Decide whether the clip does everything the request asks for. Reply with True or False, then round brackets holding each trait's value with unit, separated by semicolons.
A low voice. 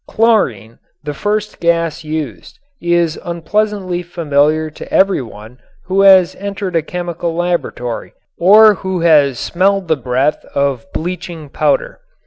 False (170 Hz)